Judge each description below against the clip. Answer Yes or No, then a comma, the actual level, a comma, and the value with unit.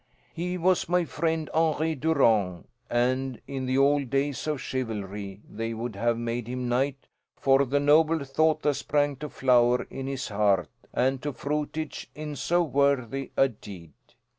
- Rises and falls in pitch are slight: No, average, 3.9 semitones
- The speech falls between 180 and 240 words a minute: No, average, 160 wpm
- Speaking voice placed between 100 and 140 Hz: Yes, low, 135 Hz